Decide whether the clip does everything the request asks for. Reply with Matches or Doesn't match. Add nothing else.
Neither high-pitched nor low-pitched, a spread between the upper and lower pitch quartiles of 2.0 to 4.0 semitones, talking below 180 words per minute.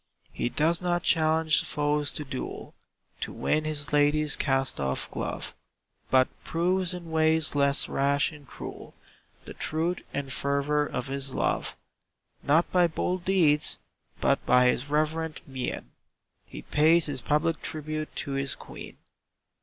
Matches